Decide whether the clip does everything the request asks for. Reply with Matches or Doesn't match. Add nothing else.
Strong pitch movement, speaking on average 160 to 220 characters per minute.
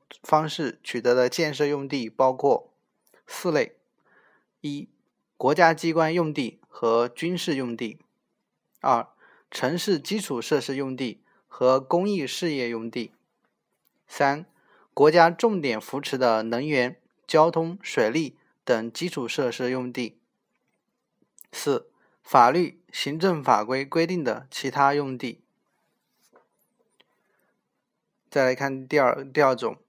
Doesn't match